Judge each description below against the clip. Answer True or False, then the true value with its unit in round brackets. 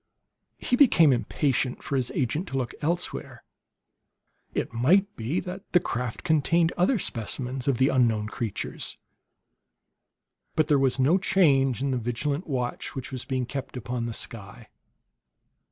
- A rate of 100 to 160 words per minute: True (145 wpm)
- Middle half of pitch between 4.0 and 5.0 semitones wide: True (4.5 semitones)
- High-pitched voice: False (135 Hz)